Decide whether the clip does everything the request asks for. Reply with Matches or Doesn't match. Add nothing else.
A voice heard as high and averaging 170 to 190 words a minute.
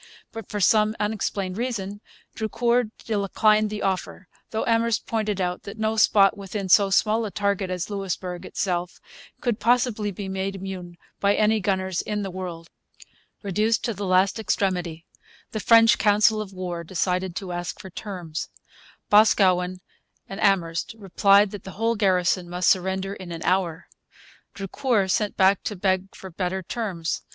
Doesn't match